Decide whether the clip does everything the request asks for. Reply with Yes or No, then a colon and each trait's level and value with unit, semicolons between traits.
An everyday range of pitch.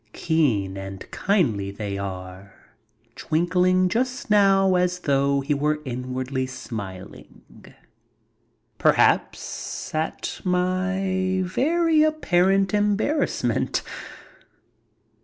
No: wide, 7.3 semitones